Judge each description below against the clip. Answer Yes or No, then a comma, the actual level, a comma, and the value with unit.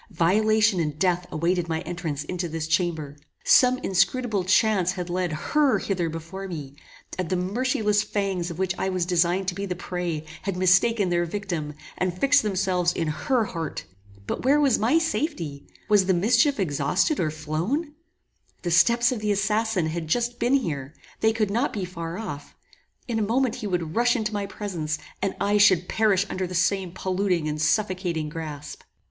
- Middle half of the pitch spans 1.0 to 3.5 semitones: No, average, 4.2 semitones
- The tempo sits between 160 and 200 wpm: Yes, average, 180 wpm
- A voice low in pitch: No, medium, 185 Hz